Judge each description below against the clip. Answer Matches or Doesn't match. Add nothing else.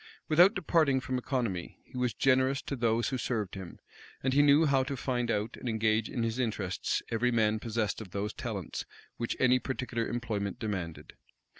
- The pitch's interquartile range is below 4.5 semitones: Matches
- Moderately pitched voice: Doesn't match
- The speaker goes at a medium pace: Matches